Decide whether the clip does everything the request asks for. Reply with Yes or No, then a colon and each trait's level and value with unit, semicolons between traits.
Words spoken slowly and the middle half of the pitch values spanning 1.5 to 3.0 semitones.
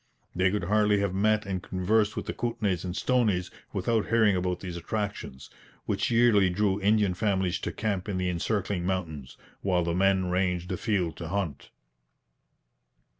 No: average, 160 wpm; average, 2.7 semitones